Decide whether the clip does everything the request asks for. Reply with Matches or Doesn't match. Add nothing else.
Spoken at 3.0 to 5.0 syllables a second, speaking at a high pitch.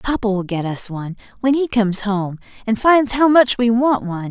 Doesn't match